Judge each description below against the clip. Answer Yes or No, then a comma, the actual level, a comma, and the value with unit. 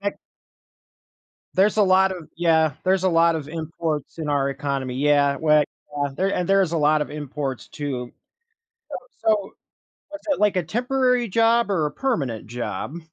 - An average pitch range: Yes, average, 5.0 semitones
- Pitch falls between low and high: Yes, medium, 165 Hz